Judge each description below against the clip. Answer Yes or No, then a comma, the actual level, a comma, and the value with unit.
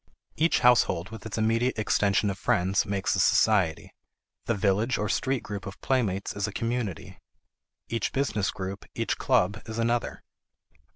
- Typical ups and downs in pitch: Yes, average, 3.1 semitones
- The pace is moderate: Yes, average, 155 wpm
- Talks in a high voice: No, low, 105 Hz